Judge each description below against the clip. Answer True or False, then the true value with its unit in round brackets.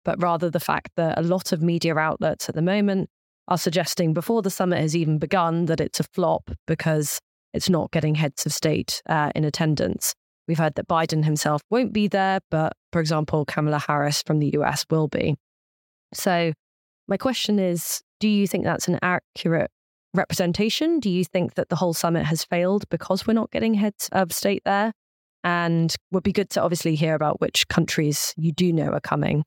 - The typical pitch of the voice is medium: True (170 Hz)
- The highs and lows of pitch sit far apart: False (3.3 semitones)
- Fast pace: False (195 wpm)